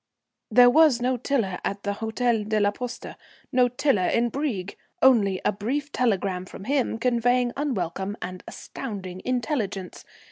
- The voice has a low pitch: No, high, 230 Hz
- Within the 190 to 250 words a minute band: No, average, 145 wpm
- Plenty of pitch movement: No, average, 4.2 semitones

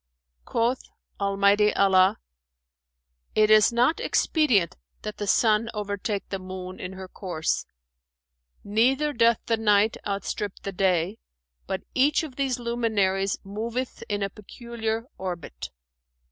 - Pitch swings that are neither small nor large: Yes, average, 3.3 semitones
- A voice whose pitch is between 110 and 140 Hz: No, high, 210 Hz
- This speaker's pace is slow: Yes, slow, 120 wpm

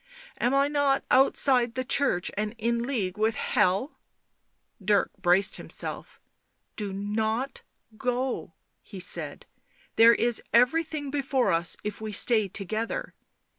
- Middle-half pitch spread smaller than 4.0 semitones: No, average, 4.4 semitones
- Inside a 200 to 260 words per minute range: No, slow, 135 wpm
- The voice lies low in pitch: No, high, 230 Hz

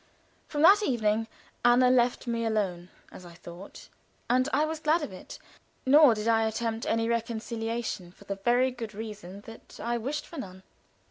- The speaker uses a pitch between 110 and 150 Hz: No, high, 230 Hz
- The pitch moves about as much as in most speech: Yes, average, 3.3 semitones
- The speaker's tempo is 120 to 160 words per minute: No, average, 175 wpm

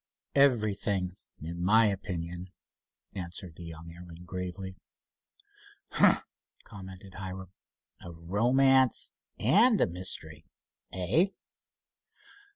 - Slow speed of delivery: Yes, slow, 85 wpm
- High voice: No, very low, 95 Hz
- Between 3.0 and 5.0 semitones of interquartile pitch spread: Yes, average, 3.5 semitones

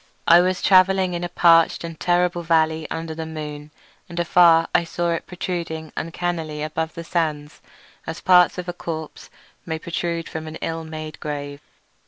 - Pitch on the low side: No, medium, 165 Hz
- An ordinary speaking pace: Yes, average, 170 wpm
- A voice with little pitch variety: Yes, narrow, 1.6 semitones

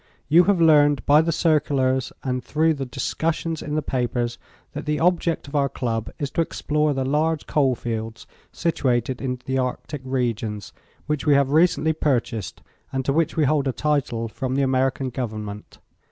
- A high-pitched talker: No, low, 135 Hz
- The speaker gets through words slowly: No, average, 175 wpm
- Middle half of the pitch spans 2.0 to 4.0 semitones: Yes, average, 3.4 semitones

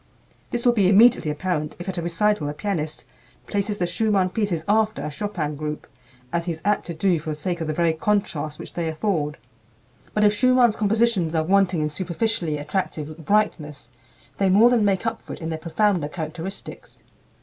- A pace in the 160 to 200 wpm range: Yes, average, 195 wpm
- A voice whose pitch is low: No, medium, 180 Hz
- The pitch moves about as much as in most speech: Yes, average, 4.9 semitones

